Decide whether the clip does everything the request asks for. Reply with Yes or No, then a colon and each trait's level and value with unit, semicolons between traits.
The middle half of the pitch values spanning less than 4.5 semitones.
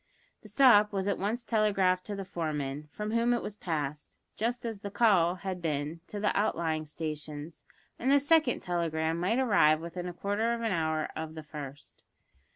No: average, 5.2 semitones